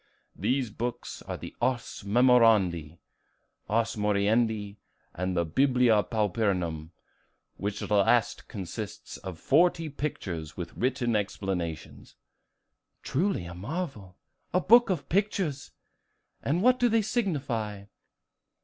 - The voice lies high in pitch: No, low, 110 Hz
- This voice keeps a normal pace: No, slow, 105 wpm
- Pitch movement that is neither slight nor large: No, wide, 6.4 semitones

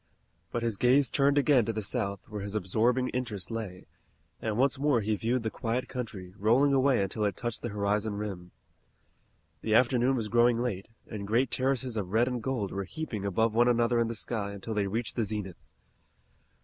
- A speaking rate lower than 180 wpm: No, average, 195 wpm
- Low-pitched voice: Yes, low, 115 Hz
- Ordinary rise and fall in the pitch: Yes, average, 3.3 semitones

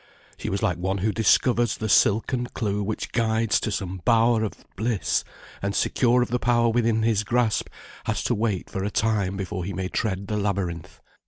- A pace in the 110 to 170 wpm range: No, average, 190 wpm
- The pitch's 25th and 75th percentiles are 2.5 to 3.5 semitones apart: Yes, average, 2.8 semitones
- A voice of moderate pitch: No, low, 110 Hz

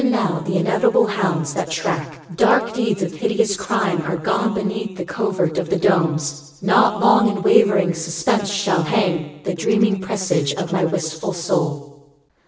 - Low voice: No, medium, 185 Hz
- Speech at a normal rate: Yes, average, 165 wpm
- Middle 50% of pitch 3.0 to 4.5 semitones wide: Yes, average, 4.1 semitones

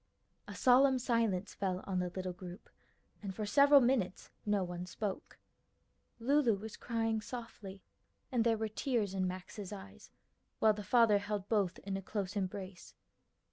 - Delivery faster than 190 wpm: No, average, 155 wpm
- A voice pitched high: Yes, high, 205 Hz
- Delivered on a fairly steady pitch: No, average, 3.5 semitones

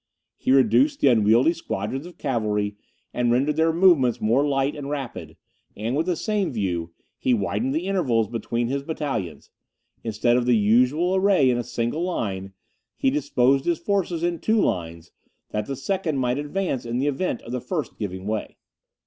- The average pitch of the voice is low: Yes, low, 130 Hz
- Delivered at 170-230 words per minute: Yes, average, 175 wpm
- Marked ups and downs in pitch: Yes, wide, 6.1 semitones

